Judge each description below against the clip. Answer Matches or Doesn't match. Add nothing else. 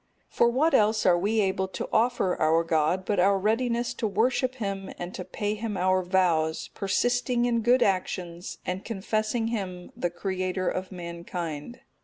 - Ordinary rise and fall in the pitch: Matches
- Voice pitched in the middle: Doesn't match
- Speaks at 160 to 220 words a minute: Matches